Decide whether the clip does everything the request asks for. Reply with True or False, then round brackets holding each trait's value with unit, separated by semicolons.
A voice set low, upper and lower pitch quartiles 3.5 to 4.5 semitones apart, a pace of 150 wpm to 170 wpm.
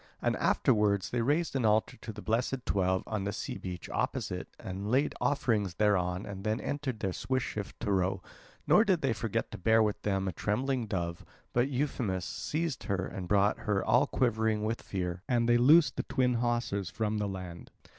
False (105 Hz; 4.0 semitones; 195 wpm)